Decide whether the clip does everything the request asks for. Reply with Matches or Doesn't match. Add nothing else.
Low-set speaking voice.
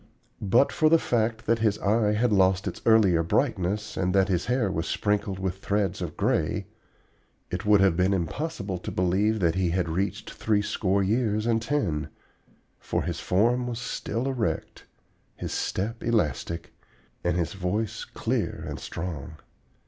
Matches